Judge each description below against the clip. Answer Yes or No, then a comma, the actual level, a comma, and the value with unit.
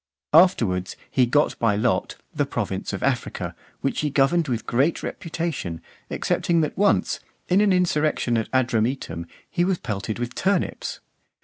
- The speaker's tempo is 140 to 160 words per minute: Yes, average, 145 wpm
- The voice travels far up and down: Yes, wide, 7.0 semitones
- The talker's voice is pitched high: No, low, 135 Hz